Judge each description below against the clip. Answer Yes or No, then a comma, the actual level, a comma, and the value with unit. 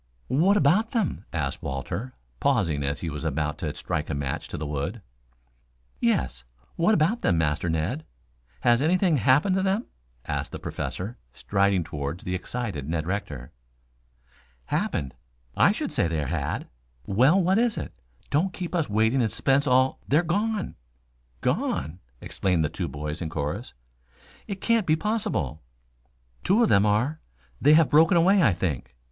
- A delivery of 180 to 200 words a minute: No, average, 165 wpm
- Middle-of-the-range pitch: No, low, 110 Hz